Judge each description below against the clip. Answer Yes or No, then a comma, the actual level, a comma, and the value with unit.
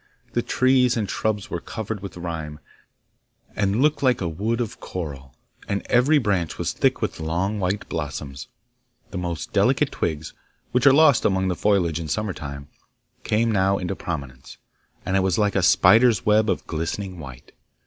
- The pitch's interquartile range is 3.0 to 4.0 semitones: No, average, 4.8 semitones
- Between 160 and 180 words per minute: Yes, average, 170 wpm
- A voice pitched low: Yes, very low, 95 Hz